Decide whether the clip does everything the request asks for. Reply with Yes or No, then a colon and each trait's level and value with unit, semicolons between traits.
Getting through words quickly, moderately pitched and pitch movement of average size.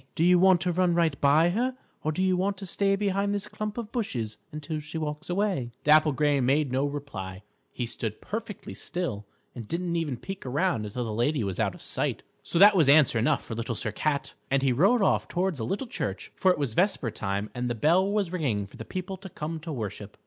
No: fast, 230 wpm; medium, 155 Hz; wide, 7.2 semitones